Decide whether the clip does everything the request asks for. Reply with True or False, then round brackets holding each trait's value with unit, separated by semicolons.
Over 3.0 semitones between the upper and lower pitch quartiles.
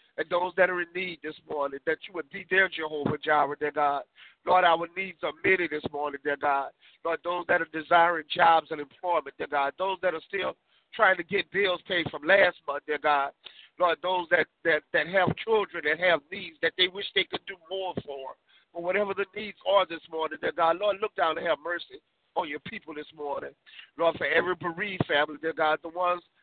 True (3.5 semitones)